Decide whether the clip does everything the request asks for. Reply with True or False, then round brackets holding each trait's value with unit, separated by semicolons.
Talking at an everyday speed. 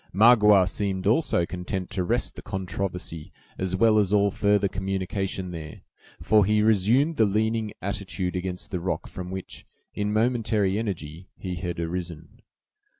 True (150 wpm)